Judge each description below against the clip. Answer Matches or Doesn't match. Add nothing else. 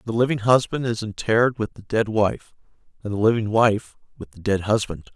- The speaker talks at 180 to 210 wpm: Matches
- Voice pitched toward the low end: Matches